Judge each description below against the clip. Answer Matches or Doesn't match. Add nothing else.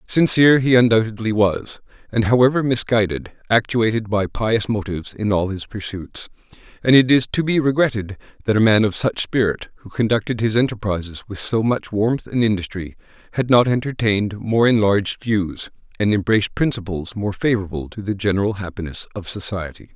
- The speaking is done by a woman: Doesn't match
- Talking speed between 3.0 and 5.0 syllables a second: Doesn't match